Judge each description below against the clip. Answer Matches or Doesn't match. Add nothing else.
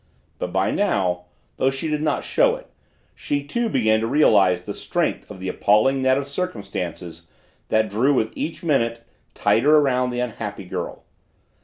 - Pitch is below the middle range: Matches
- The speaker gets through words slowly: Doesn't match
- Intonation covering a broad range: Matches